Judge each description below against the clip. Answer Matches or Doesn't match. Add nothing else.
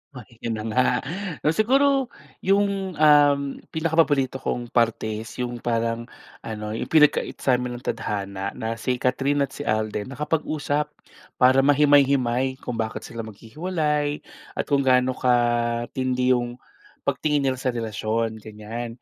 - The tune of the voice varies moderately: Matches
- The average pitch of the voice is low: Matches